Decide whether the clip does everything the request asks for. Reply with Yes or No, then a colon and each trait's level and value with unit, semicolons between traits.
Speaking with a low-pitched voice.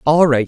No: medium, 145 Hz